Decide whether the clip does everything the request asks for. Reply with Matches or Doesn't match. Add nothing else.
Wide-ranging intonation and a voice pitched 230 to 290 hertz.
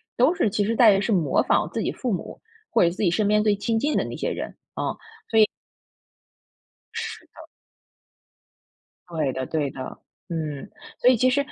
Doesn't match